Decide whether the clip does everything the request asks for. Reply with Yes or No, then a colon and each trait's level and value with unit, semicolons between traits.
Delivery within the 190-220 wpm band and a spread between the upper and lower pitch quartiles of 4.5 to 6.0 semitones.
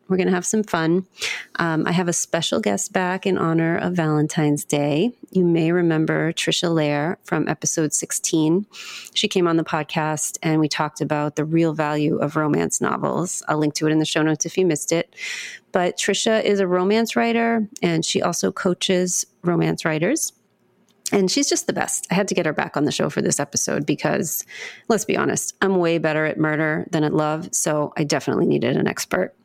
No: fast, 205 wpm; average, 3.3 semitones